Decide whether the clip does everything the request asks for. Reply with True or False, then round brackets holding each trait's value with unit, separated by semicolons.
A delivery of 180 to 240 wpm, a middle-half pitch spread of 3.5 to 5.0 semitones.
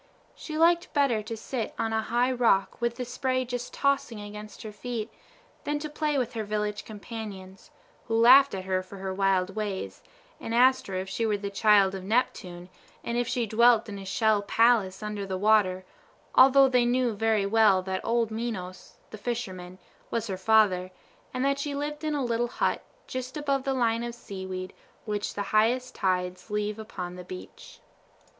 True (185 wpm; 4.1 semitones)